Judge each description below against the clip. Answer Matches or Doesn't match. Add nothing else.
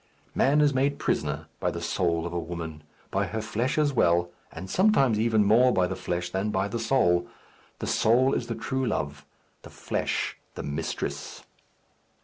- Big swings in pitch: Matches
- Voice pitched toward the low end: Matches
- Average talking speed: Matches